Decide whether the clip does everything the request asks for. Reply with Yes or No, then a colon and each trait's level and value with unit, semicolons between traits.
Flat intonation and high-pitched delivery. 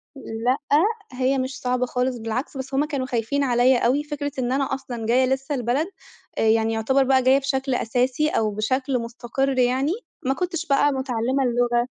Yes: narrow, 2.1 semitones; very high, 260 Hz